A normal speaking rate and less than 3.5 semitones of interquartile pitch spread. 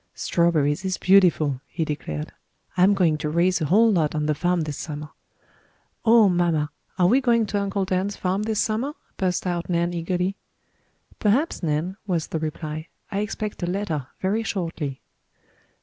No: average, 165 wpm; average, 4.2 semitones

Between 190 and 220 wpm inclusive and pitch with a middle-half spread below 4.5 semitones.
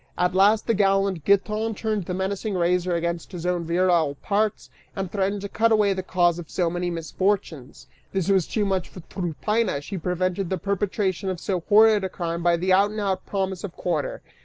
Yes: average, 200 wpm; narrow, 2.5 semitones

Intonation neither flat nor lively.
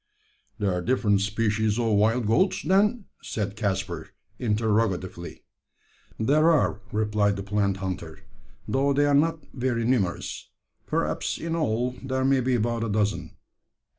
Yes: average, 4.4 semitones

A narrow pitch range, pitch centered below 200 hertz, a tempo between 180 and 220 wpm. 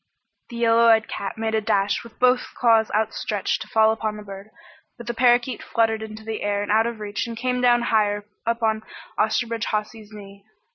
No: narrow, 1.7 semitones; high, 220 Hz; average, 200 wpm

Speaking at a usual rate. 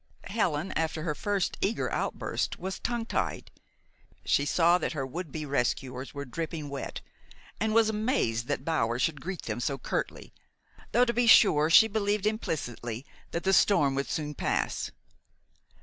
Yes: average, 160 wpm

